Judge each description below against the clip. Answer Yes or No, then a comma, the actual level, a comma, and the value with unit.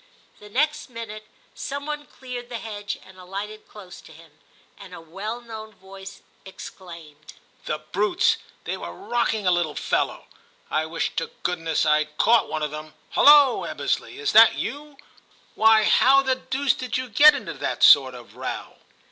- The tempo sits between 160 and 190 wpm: Yes, average, 175 wpm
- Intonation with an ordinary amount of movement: No, wide, 6.5 semitones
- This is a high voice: Yes, high, 210 Hz